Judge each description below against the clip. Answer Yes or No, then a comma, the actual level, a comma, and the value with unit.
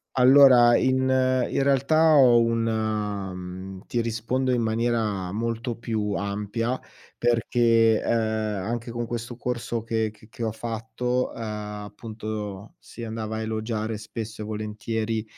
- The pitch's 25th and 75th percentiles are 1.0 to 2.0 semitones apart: Yes, narrow, 1.7 semitones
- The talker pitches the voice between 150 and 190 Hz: No, low, 115 Hz